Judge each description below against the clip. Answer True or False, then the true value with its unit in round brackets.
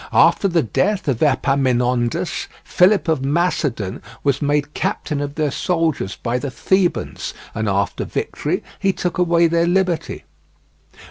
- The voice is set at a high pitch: False (150 Hz)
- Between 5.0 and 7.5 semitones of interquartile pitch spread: True (5.4 semitones)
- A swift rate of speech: False (135 wpm)